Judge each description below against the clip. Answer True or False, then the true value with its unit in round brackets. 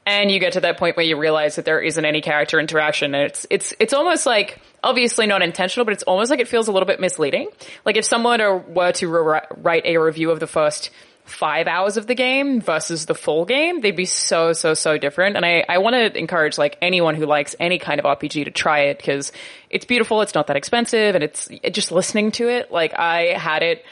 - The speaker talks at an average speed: False (240 wpm)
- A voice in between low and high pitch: True (175 Hz)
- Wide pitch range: True (5.8 semitones)